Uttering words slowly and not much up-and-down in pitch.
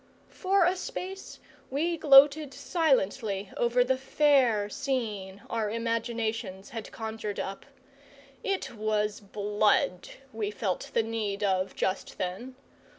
No: slow, 115 wpm; average, 4.7 semitones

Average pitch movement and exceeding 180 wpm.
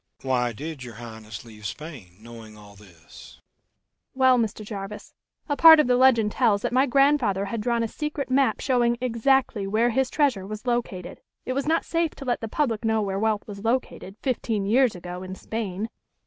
No: wide, 6.1 semitones; average, 190 wpm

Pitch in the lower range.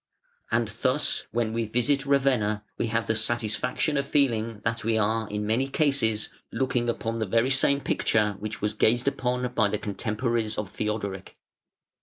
Yes: low, 115 Hz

